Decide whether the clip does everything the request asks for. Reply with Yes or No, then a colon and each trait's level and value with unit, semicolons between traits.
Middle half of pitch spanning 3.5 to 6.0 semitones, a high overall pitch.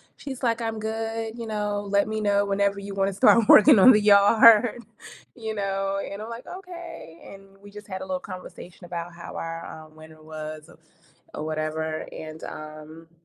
Yes: average, 5.0 semitones; high, 200 Hz